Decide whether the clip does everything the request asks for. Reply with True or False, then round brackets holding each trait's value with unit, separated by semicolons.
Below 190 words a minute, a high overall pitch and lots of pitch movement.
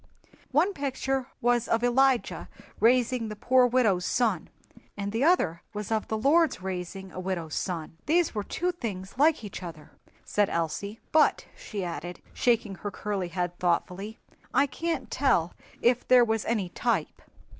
True (155 wpm; 220 Hz; 5.7 semitones)